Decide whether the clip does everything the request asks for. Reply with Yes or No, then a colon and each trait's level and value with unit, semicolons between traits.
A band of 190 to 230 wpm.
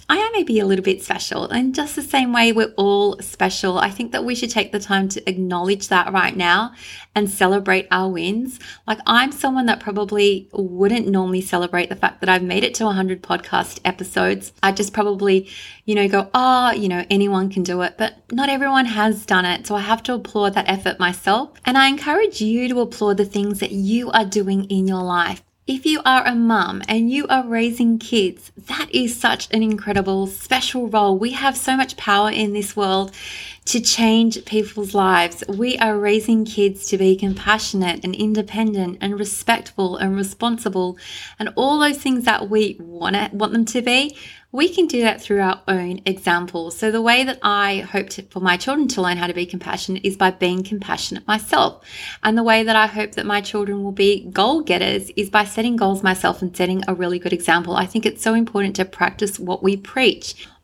Yes: fast, 205 wpm